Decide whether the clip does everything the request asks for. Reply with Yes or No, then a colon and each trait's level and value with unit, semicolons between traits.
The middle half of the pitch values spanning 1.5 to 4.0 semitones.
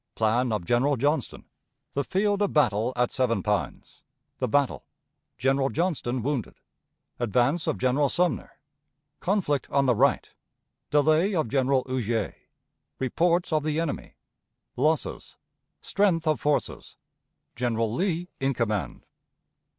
No: average, 4.7 semitones